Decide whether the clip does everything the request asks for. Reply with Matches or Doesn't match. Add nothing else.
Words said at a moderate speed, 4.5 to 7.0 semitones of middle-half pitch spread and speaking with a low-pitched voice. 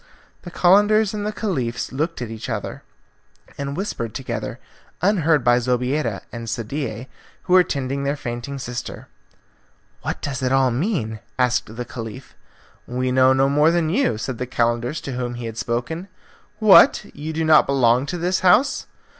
Matches